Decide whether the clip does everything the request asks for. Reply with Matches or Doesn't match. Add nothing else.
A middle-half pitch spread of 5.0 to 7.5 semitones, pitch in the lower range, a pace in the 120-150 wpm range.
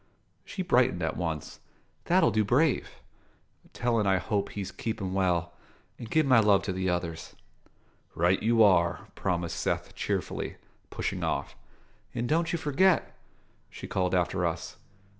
Matches